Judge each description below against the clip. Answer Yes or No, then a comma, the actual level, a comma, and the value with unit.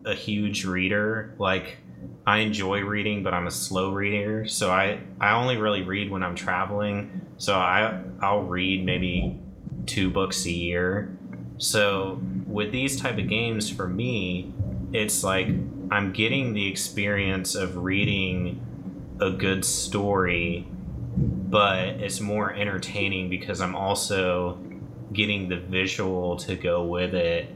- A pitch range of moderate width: No, narrow, 2.0 semitones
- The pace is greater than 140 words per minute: No, slow, 135 wpm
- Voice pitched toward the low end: Yes, very low, 95 Hz